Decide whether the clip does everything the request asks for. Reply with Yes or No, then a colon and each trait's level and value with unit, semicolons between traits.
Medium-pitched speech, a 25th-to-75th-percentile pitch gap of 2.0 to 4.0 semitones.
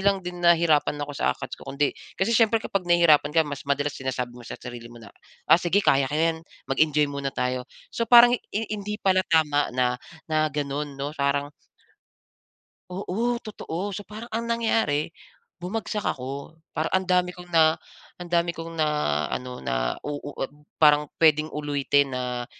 No: medium, 155 Hz; average, 4.4 semitones